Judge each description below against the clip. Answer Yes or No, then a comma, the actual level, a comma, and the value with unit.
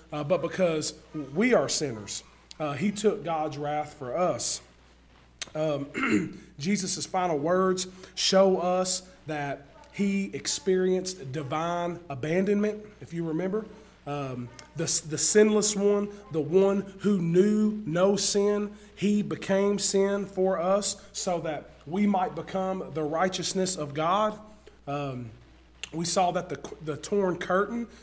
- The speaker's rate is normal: No, slow, 130 wpm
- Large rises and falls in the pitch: No, average, 4.5 semitones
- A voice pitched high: No, medium, 180 Hz